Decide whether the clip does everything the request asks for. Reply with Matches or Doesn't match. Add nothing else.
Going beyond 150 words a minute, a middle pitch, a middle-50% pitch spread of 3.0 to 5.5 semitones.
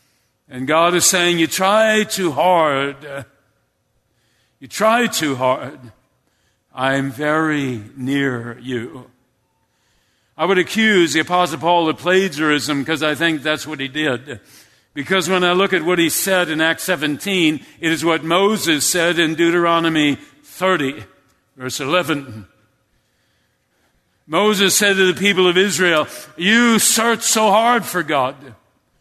Doesn't match